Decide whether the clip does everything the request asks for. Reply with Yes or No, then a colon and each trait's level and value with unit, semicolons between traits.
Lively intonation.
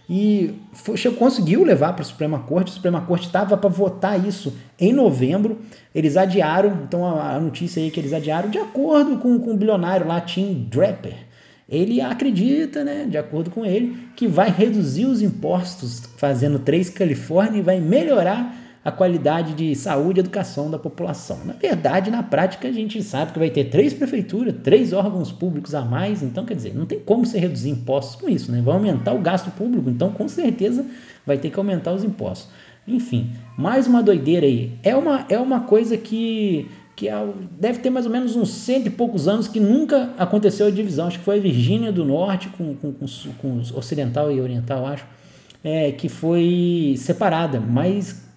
Yes: wide, 5.7 semitones